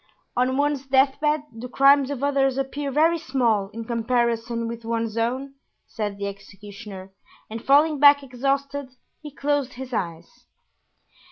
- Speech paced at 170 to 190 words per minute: No, average, 145 wpm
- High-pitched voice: Yes, very high, 260 Hz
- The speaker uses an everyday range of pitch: Yes, average, 3.6 semitones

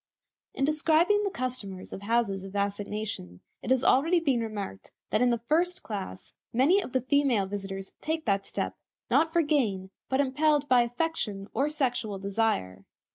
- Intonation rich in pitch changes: Yes, wide, 6.9 semitones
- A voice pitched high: Yes, high, 240 Hz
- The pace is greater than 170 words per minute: No, average, 165 wpm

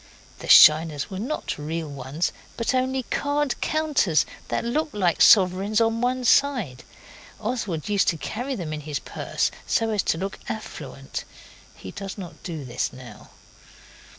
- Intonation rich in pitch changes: Yes, wide, 7.8 semitones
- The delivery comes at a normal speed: Yes, average, 150 wpm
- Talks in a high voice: Yes, high, 195 Hz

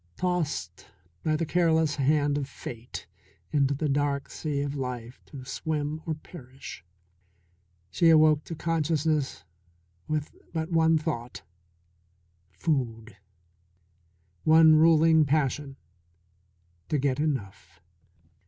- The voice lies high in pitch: No, medium, 150 Hz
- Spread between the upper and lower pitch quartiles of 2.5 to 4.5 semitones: Yes, average, 2.9 semitones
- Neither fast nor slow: No, slow, 105 wpm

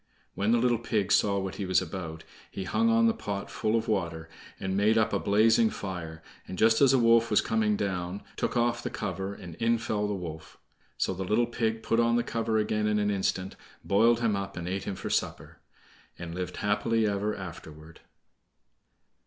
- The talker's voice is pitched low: Yes, low, 105 Hz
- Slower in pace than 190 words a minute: No, average, 200 wpm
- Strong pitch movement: No, average, 3.3 semitones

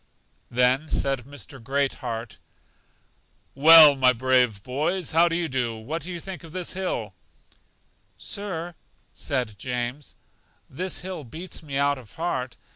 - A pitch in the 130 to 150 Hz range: Yes, medium, 140 Hz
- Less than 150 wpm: Yes, slow, 135 wpm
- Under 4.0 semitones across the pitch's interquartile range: No, average, 4.9 semitones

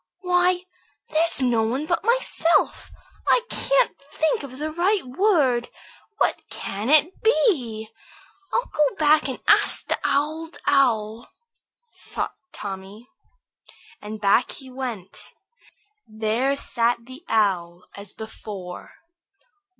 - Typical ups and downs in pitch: No, wide, 6.5 semitones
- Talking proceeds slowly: Yes, slow, 110 wpm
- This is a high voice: Yes, very high, 260 Hz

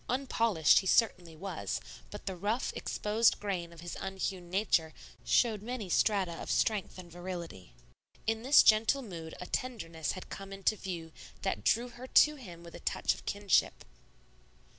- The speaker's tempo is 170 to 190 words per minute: No, average, 160 wpm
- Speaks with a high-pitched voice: Yes, high, 195 Hz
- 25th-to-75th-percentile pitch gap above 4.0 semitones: Yes, average, 4.5 semitones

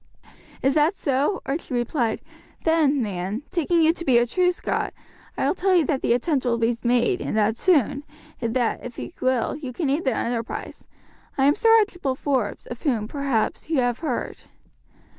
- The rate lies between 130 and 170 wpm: No, average, 190 wpm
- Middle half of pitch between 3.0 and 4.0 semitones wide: No, average, 4.9 semitones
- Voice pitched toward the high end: Yes, very high, 265 Hz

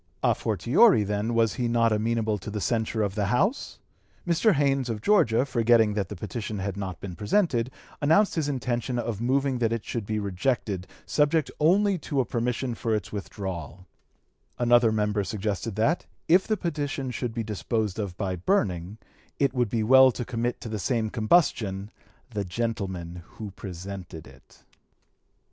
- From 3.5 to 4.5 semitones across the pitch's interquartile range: Yes, average, 4.1 semitones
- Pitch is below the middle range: Yes, low, 115 Hz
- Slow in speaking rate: No, average, 165 wpm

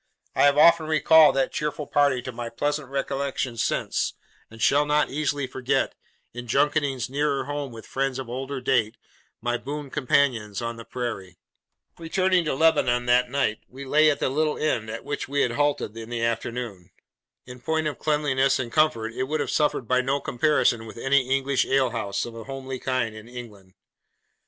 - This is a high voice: No, low, 135 Hz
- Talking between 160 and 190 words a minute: Yes, average, 180 wpm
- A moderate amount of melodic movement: Yes, average, 3.5 semitones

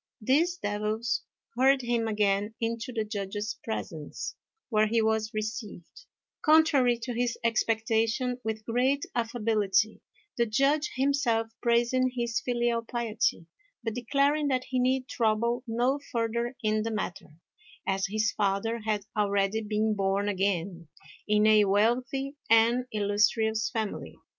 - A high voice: Yes, high, 225 Hz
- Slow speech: Yes, slow, 130 wpm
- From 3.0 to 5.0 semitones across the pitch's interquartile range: No, narrow, 2.6 semitones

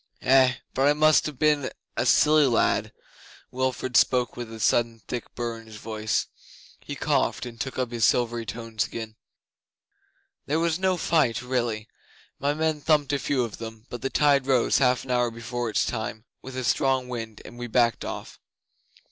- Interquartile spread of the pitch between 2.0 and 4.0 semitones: Yes, average, 3.0 semitones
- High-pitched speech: No, low, 125 Hz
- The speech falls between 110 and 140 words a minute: No, average, 180 wpm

